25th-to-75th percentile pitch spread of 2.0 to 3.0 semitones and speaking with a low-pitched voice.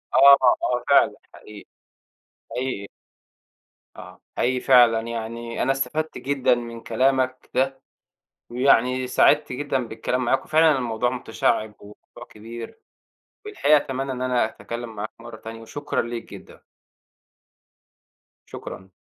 Yes: narrow, 2.6 semitones; low, 125 Hz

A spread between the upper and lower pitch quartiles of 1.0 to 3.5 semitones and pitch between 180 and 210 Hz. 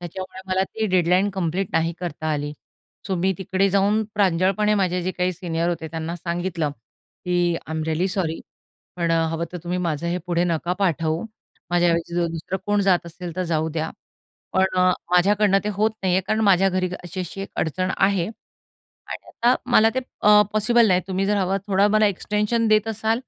Yes: average, 2.7 semitones; medium, 185 Hz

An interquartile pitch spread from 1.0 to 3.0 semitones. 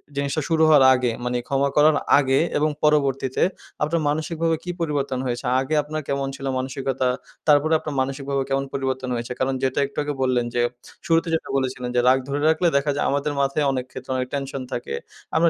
Yes: narrow, 2.4 semitones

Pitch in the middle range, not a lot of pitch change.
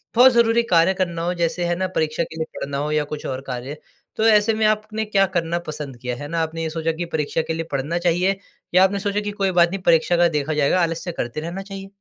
No: medium, 170 Hz; average, 3.8 semitones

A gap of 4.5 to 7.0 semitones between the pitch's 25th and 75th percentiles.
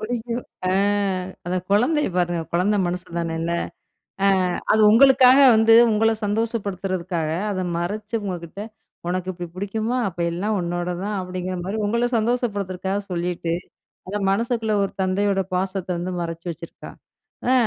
No: average, 3.7 semitones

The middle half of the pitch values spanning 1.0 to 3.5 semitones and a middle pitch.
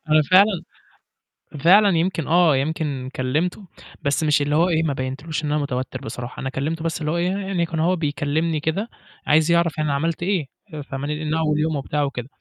Yes: average, 2.9 semitones; medium, 155 Hz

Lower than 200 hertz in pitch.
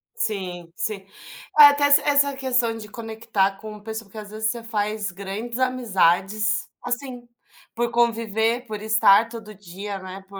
No: high, 220 Hz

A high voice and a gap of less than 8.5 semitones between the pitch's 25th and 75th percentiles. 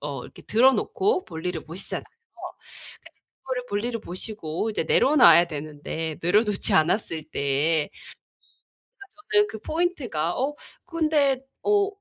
No: high, 210 Hz; wide, 8.8 semitones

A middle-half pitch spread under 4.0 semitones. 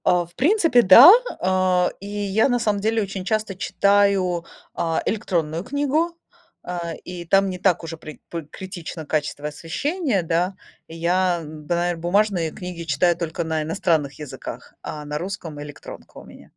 Yes: average, 3.6 semitones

